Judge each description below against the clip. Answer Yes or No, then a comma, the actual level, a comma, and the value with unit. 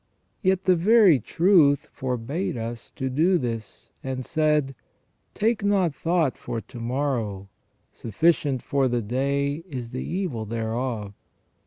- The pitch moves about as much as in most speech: No, wide, 6.0 semitones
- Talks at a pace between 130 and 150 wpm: Yes, slow, 135 wpm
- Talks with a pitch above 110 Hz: Yes, low, 135 Hz